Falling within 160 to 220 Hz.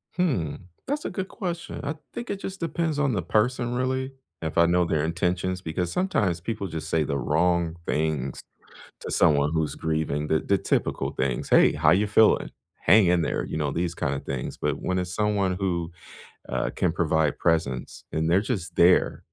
No: very low, 90 Hz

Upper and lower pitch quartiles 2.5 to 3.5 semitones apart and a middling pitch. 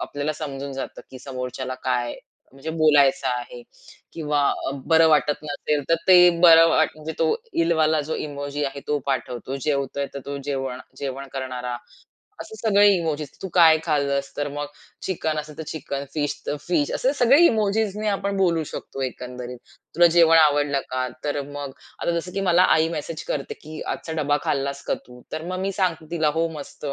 Yes: average, 3.2 semitones; medium, 150 Hz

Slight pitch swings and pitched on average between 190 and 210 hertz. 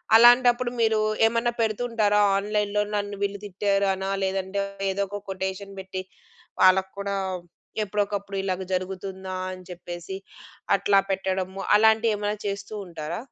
Yes: narrow, 1.7 semitones; high, 200 Hz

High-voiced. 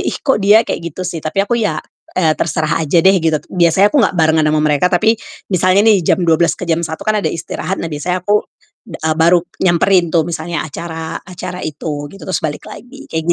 No: medium, 170 Hz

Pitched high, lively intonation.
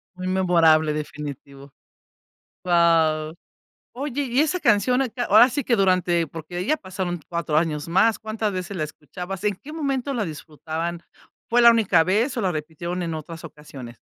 No: medium, 180 Hz; wide, 5.8 semitones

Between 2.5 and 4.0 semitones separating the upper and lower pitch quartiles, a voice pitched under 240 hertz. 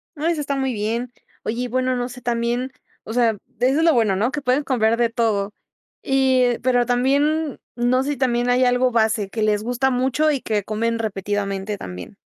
No: average, 2.8 semitones; high, 245 Hz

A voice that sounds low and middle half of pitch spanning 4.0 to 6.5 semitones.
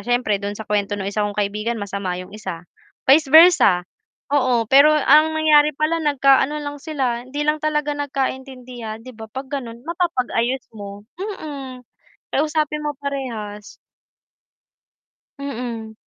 No: very high, 260 Hz; average, 5.2 semitones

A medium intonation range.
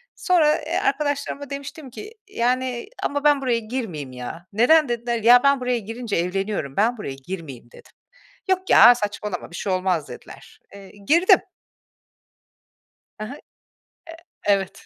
No: wide, 6.3 semitones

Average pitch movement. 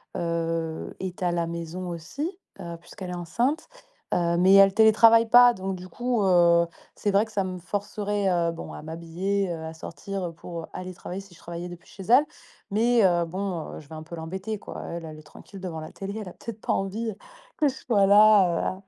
Yes: average, 3.3 semitones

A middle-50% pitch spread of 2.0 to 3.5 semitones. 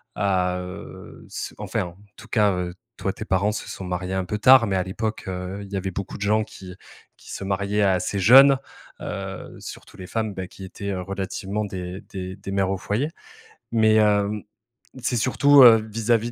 Yes: narrow, 2.5 semitones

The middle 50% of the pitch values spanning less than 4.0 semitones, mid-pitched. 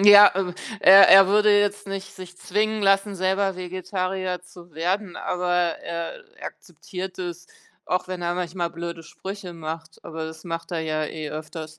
Yes: narrow, 2.6 semitones; medium, 180 Hz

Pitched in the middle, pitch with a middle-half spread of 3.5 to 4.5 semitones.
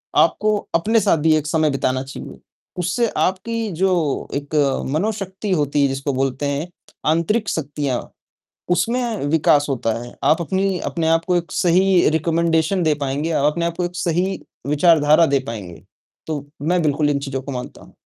Yes: medium, 160 Hz; average, 4.2 semitones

